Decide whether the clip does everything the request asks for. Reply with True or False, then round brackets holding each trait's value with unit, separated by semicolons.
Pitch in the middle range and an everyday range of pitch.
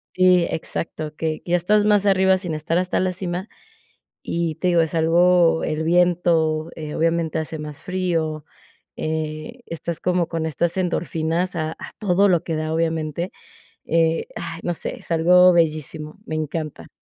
False (165 Hz; 2.2 semitones)